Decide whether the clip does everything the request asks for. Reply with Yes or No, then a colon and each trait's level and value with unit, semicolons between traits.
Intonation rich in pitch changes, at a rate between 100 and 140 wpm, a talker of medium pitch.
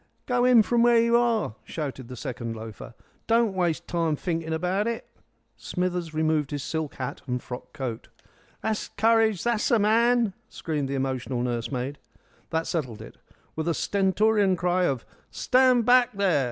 No: wide, 8.4 semitones; average, 160 wpm; medium, 175 Hz